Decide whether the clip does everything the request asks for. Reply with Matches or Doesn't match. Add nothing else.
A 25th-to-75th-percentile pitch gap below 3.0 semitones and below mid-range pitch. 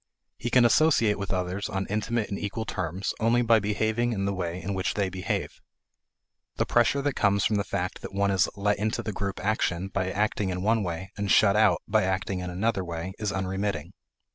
Matches